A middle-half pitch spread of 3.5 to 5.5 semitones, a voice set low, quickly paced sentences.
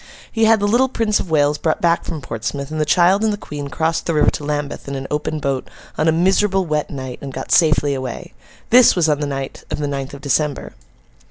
No: average, 4.0 semitones; medium, 150 Hz; fast, 240 wpm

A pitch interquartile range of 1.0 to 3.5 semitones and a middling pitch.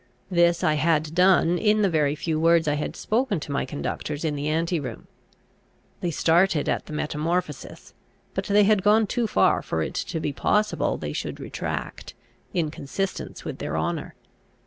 No: average, 4.2 semitones; medium, 165 Hz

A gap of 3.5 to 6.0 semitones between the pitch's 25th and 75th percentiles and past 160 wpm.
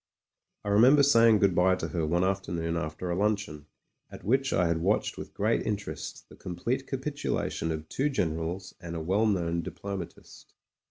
Yes: average, 4.3 semitones; average, 170 wpm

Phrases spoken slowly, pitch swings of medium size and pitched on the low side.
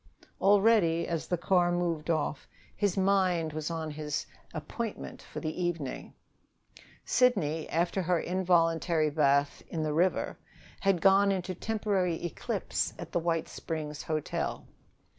No: slow, 130 wpm; average, 3.1 semitones; medium, 170 Hz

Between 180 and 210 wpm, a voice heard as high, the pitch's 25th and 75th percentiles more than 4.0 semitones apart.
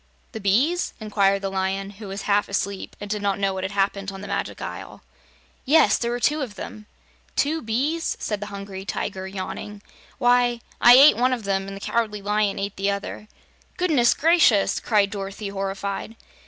No: average, 185 wpm; high, 205 Hz; average, 3.3 semitones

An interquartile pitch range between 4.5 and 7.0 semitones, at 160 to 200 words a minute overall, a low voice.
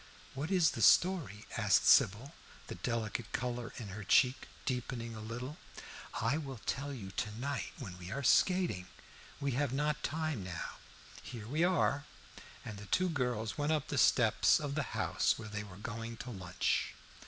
Yes: average, 5.0 semitones; average, 175 wpm; low, 125 Hz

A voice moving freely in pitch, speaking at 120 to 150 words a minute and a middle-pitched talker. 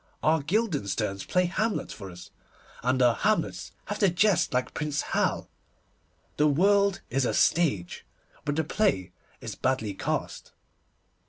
Yes: wide, 7.7 semitones; average, 140 wpm; medium, 145 Hz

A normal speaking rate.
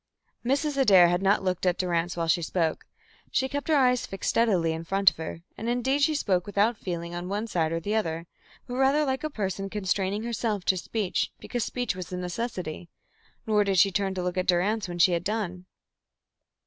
No: fast, 210 wpm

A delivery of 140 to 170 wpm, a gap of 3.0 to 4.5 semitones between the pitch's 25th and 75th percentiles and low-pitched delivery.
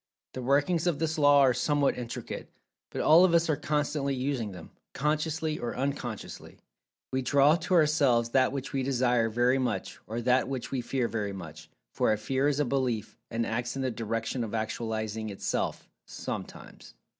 No: average, 180 wpm; average, 3.9 semitones; low, 130 Hz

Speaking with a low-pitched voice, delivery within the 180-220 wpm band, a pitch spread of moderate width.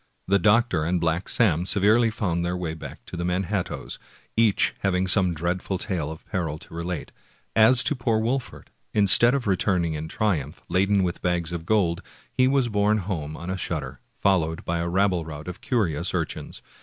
Yes: very low, 90 Hz; average, 195 wpm; average, 3.8 semitones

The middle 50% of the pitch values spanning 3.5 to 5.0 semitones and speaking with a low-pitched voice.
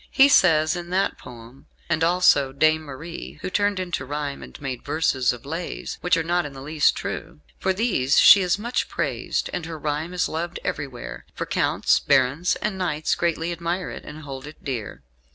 No: average, 4.2 semitones; medium, 160 Hz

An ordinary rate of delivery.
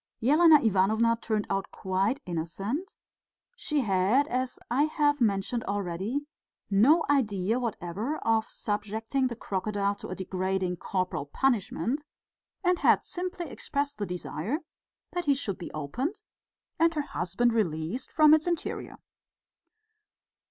No: slow, 125 wpm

